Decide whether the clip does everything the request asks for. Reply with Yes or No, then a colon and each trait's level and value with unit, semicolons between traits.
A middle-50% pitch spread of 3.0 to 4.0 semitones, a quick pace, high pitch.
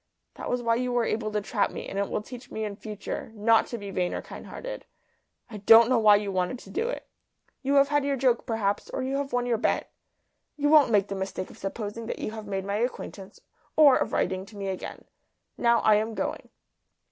Yes: average, 3.6 semitones; fast, 235 wpm; high, 225 Hz